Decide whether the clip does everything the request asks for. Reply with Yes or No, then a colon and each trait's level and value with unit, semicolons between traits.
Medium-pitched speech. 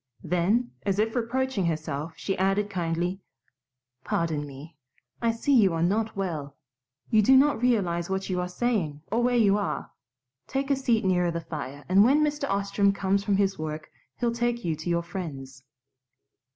No: high, 195 Hz